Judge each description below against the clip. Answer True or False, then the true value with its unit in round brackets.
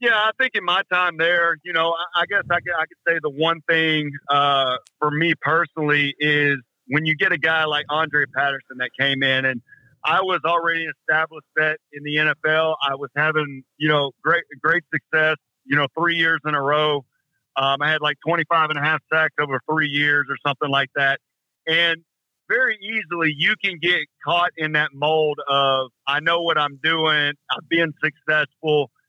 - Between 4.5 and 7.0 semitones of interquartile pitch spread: False (2.4 semitones)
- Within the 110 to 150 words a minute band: False (195 wpm)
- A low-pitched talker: False (155 Hz)